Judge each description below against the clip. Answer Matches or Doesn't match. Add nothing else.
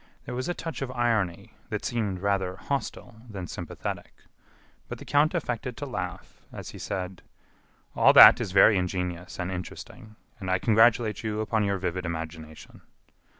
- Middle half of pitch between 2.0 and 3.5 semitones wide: Doesn't match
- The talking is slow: Doesn't match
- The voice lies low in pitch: Matches